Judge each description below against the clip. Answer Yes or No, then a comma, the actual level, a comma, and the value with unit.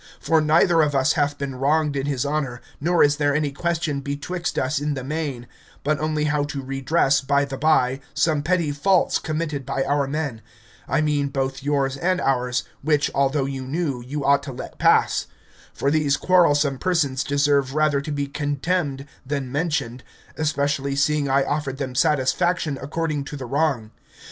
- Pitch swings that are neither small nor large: No, narrow, 2.0 semitones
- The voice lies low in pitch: No, medium, 145 Hz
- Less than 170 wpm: No, average, 175 wpm